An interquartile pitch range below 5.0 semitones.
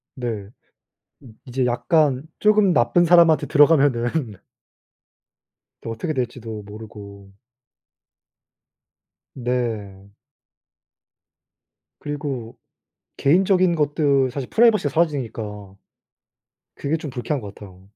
No: wide, 5.5 semitones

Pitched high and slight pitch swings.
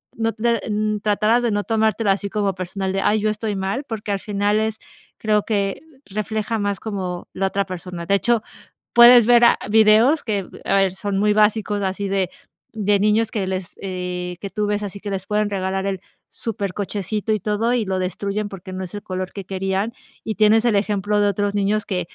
Yes: high, 205 Hz; narrow, 1.9 semitones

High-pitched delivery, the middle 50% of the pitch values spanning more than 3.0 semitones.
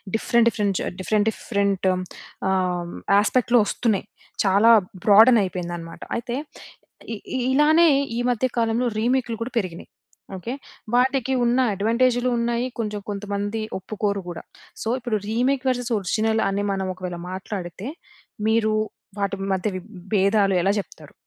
Yes: high, 215 Hz; average, 3.5 semitones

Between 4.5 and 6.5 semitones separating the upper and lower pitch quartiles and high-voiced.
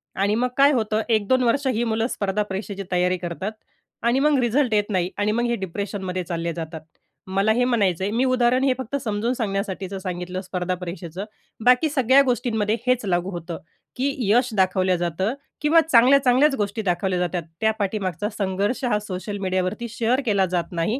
Yes: average, 4.8 semitones; high, 205 Hz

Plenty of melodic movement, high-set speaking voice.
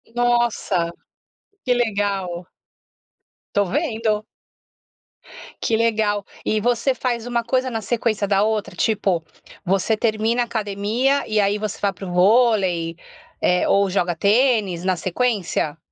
No: average, 3.3 semitones; high, 215 Hz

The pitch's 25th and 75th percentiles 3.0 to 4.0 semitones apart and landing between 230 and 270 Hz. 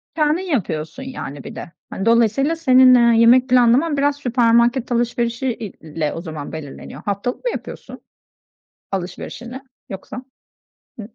No: average, 5.2 semitones; high, 235 Hz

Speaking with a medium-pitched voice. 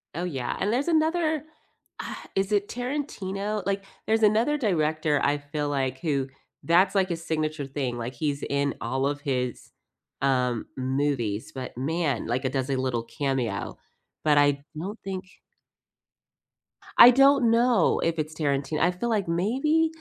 Yes: medium, 155 Hz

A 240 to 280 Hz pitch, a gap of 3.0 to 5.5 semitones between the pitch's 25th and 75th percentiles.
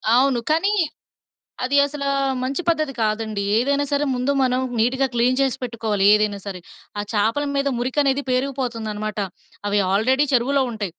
Yes: very high, 250 Hz; average, 4.2 semitones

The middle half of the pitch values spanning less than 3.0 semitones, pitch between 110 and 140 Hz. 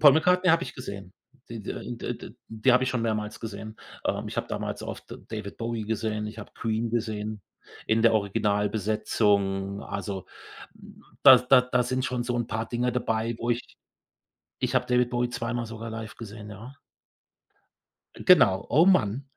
Yes: narrow, 2.6 semitones; low, 115 Hz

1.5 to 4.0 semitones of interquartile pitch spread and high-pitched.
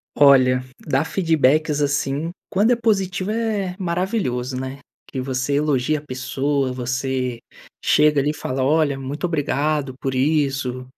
No: average, 3.6 semitones; medium, 145 Hz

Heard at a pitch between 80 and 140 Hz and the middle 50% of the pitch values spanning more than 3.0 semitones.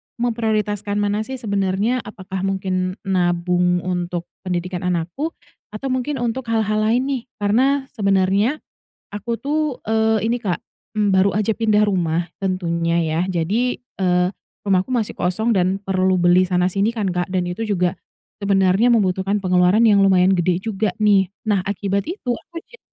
No: high, 195 Hz; average, 3.5 semitones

